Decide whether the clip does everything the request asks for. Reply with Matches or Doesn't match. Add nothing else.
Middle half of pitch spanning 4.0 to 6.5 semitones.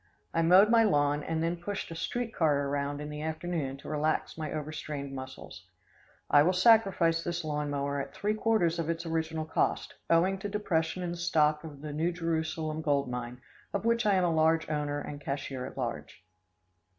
Doesn't match